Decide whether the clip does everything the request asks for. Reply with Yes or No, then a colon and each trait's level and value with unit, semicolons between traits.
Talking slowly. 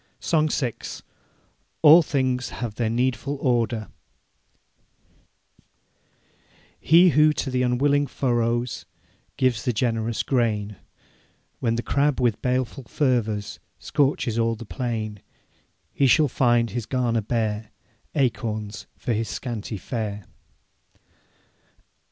Yes: slow, 105 wpm